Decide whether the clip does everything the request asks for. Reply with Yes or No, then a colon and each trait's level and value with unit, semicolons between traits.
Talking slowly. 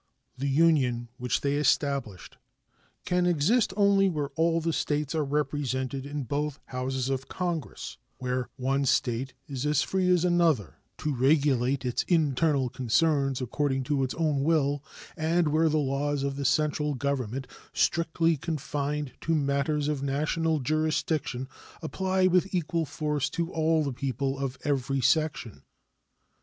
No: average, 145 wpm